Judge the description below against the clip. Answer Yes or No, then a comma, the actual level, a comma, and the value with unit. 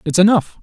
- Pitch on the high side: No, medium, 175 Hz